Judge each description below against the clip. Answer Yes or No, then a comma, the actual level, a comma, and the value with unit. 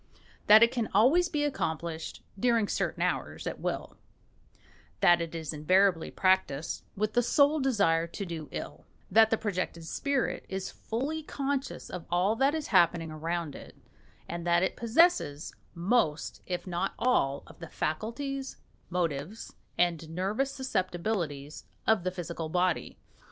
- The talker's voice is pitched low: No, medium, 185 Hz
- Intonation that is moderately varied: No, wide, 6.1 semitones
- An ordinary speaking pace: Yes, average, 145 wpm